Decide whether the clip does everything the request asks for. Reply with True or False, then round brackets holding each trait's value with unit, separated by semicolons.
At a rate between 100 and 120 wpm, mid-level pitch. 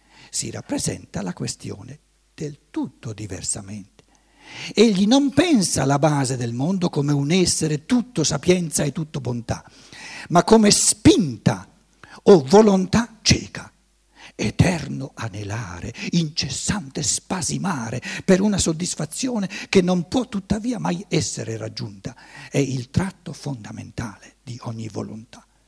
True (115 wpm; 155 Hz)